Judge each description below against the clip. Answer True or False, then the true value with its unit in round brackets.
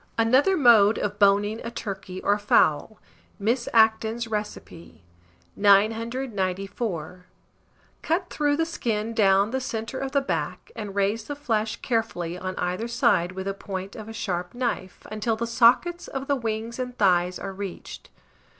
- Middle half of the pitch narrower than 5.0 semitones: True (3.3 semitones)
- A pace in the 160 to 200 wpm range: False (150 wpm)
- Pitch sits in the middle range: False (220 Hz)